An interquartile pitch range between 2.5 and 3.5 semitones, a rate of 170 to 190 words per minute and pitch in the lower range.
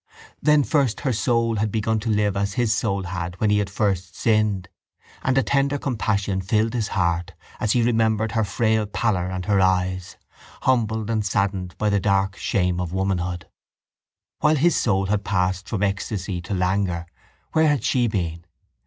Yes: average, 3.1 semitones; average, 175 wpm; low, 100 Hz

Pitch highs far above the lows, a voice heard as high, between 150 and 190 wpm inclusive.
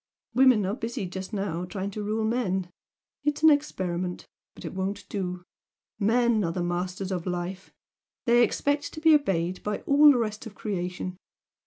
No: average, 4.6 semitones; high, 200 Hz; average, 170 wpm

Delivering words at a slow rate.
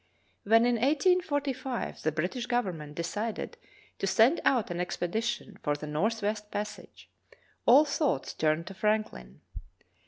Yes: slow, 125 wpm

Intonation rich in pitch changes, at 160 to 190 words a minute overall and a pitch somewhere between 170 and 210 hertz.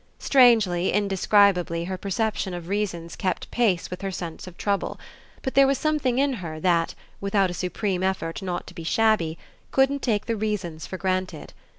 No: average, 3.7 semitones; average, 175 wpm; high, 190 Hz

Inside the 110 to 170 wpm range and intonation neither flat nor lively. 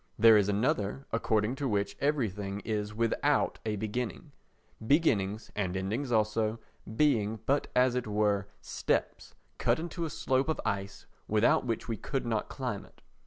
Yes: average, 150 wpm; average, 3.6 semitones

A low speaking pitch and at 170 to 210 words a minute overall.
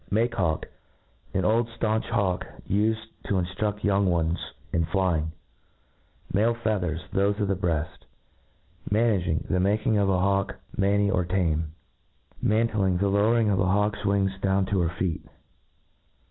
No: low, 100 Hz; average, 160 wpm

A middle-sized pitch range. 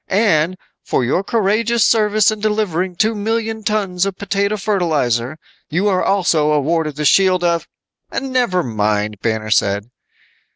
No: wide, 5.8 semitones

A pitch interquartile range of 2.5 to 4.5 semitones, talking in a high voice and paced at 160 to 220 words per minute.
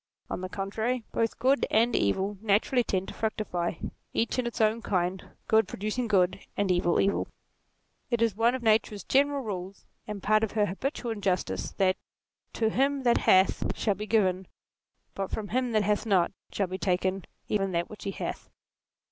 Yes: average, 3.2 semitones; high, 210 Hz; average, 180 wpm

